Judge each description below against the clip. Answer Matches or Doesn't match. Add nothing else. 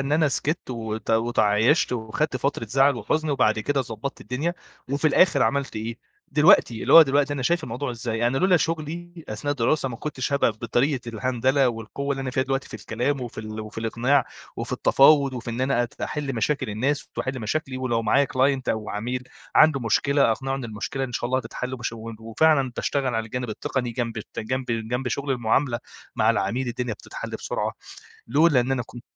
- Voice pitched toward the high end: Doesn't match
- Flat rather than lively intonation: Doesn't match